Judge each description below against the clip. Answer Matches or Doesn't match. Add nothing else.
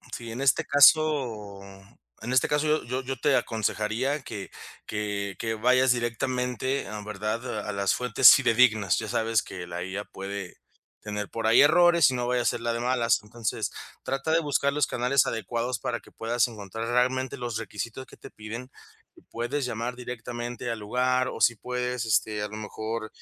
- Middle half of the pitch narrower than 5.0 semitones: Matches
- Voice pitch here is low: Matches